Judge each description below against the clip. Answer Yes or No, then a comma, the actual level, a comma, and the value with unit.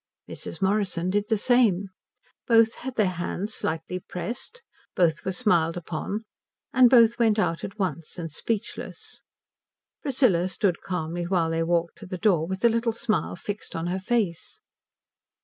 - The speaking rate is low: No, average, 155 wpm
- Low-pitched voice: No, high, 190 Hz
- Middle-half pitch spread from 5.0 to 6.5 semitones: No, average, 4.5 semitones